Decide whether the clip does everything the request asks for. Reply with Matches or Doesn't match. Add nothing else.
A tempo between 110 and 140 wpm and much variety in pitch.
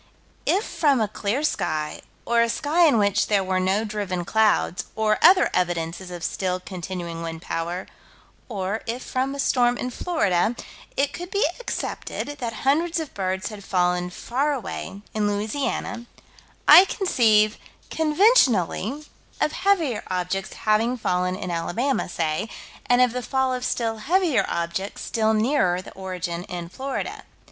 Doesn't match